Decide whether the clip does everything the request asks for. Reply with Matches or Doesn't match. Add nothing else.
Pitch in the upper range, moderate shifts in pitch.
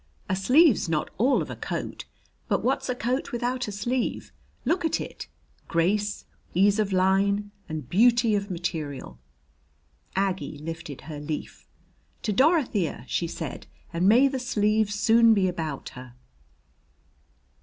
Doesn't match